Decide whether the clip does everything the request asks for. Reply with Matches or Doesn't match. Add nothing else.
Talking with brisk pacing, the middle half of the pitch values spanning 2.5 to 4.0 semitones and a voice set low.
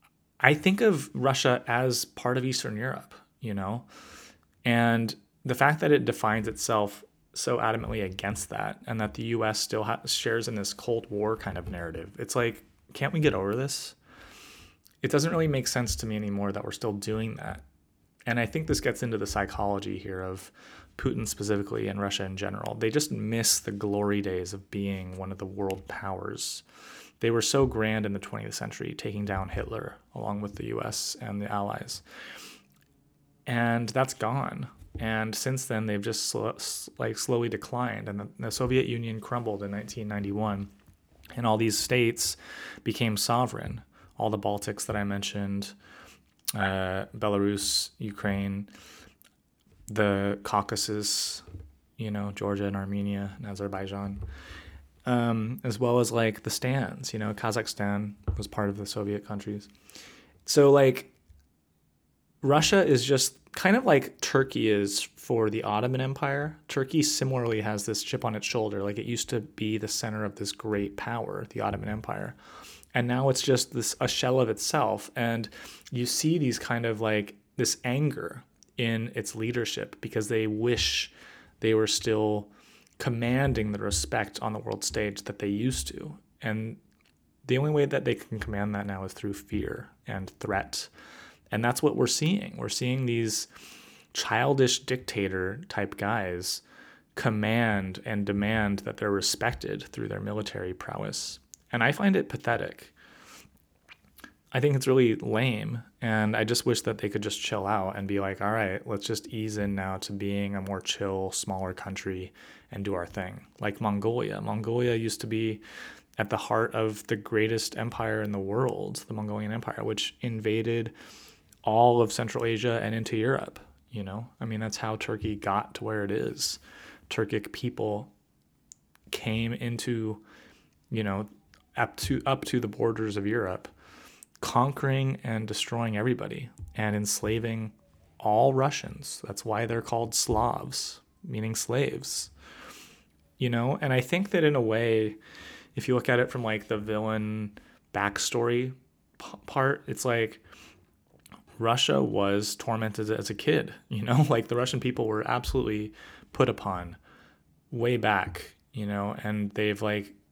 Doesn't match